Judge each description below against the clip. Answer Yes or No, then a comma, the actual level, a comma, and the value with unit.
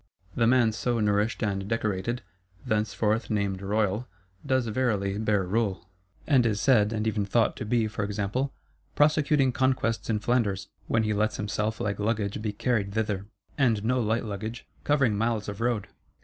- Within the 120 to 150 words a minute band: No, average, 165 wpm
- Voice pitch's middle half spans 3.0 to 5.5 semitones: No, narrow, 2.5 semitones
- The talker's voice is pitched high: No, low, 110 Hz